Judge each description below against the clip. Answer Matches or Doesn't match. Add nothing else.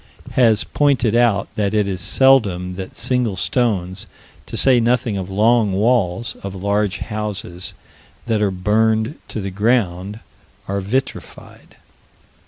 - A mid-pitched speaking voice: Doesn't match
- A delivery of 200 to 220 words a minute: Doesn't match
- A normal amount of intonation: Matches